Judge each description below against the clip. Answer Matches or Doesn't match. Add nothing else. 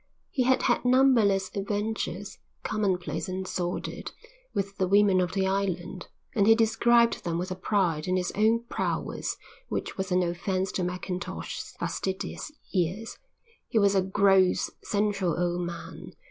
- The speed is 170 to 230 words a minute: Doesn't match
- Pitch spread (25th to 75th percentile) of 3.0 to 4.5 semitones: Doesn't match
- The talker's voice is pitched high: Matches